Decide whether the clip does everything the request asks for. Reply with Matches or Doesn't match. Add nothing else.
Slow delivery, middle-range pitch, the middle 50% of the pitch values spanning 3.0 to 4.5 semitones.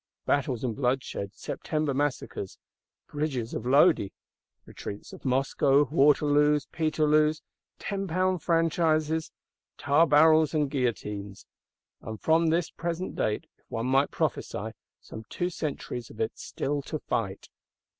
Matches